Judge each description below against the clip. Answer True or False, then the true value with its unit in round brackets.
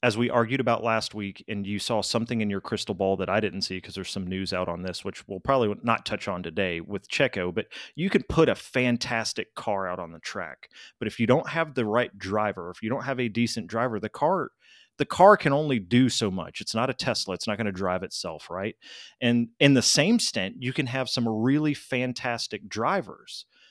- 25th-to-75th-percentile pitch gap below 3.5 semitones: False (4.3 semitones)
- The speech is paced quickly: True (235 wpm)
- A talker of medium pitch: False (115 Hz)